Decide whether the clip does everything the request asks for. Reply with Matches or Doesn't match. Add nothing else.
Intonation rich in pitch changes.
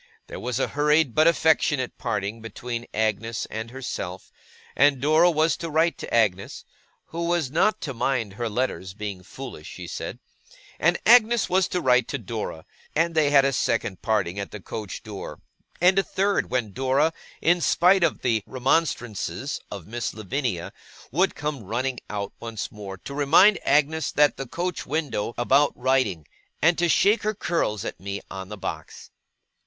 Matches